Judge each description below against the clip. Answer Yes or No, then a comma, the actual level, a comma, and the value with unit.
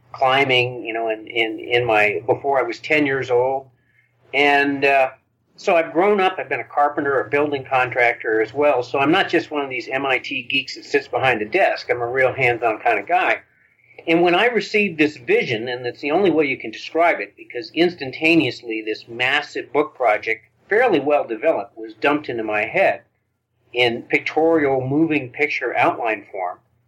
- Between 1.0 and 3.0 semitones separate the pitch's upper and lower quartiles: No, average, 3.8 semitones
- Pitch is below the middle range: Yes, low, 130 Hz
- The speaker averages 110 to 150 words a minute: No, average, 190 wpm